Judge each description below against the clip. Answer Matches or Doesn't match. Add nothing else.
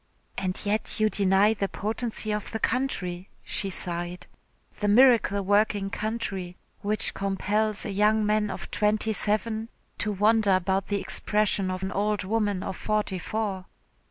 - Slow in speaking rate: Doesn't match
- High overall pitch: Matches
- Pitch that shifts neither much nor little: Doesn't match